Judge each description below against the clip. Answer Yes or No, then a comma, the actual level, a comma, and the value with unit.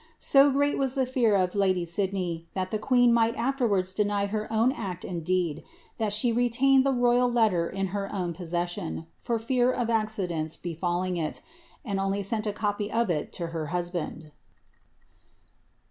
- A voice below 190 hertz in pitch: No, high, 200 Hz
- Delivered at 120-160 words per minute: No, average, 170 wpm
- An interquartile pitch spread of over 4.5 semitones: Yes, average, 4.9 semitones